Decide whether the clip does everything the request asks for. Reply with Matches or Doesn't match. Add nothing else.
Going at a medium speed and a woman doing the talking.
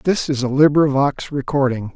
Doesn't match